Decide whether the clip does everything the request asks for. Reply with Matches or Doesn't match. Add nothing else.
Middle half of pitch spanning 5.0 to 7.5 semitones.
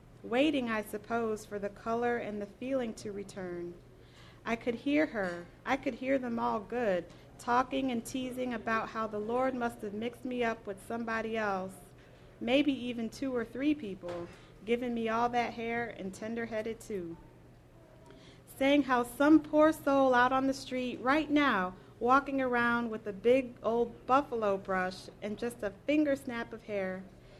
Doesn't match